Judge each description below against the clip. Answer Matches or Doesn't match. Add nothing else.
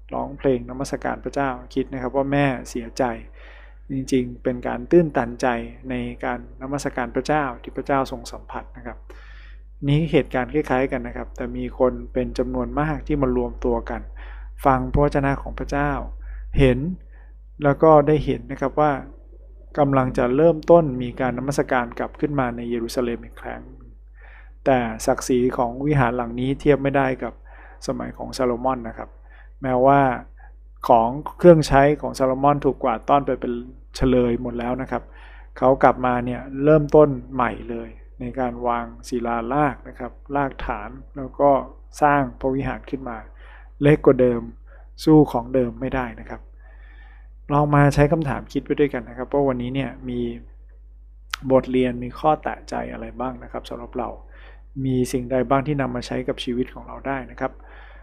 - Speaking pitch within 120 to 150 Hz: Matches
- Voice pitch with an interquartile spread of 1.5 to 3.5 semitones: Matches